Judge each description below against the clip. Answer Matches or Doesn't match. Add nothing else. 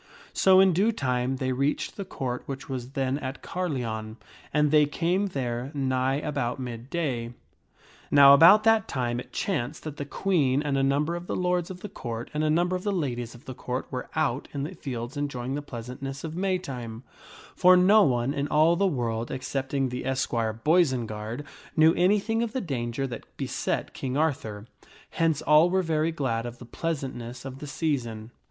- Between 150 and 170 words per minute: Doesn't match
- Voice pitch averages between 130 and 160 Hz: Matches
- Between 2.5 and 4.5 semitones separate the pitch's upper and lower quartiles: Doesn't match